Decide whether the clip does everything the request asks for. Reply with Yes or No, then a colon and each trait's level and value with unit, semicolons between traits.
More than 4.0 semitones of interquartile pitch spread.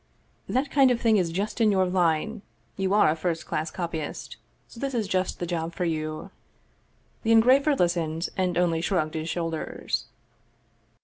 Yes: average, 5.0 semitones